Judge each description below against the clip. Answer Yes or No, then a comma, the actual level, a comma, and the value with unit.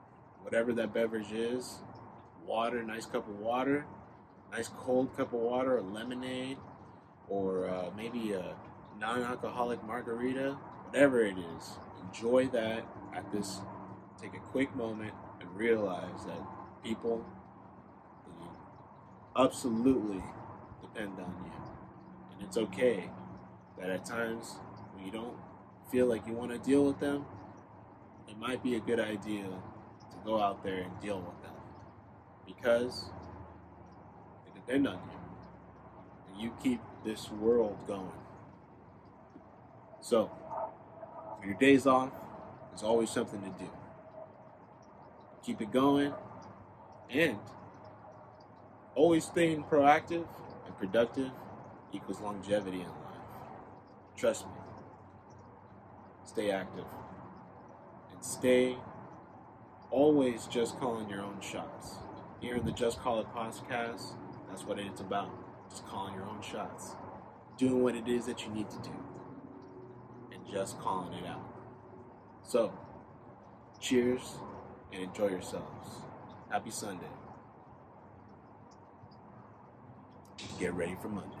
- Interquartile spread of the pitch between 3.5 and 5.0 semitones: Yes, average, 4.3 semitones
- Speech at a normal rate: No, slow, 115 wpm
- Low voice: Yes, low, 110 Hz